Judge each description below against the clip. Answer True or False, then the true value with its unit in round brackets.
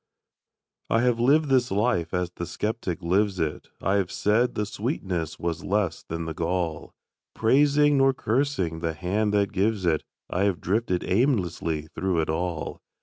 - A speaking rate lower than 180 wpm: True (160 wpm)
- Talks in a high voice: False (95 Hz)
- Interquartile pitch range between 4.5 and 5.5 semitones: True (5.2 semitones)